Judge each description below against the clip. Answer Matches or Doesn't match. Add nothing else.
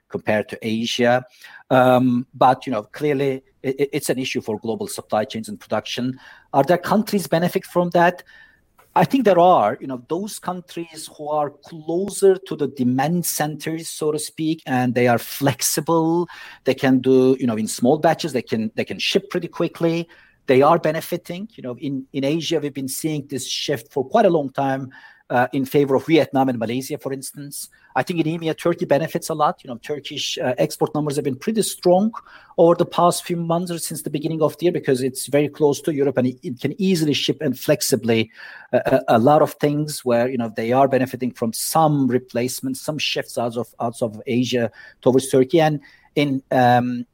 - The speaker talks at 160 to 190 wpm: Doesn't match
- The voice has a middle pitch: Matches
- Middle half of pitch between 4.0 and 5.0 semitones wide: Matches